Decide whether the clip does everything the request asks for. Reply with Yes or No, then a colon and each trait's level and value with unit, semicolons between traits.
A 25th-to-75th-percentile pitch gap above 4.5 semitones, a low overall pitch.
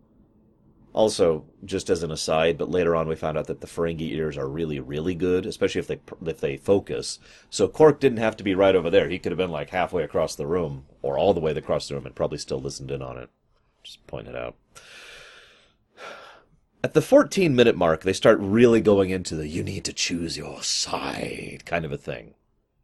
Yes: average, 5.0 semitones; very low, 85 Hz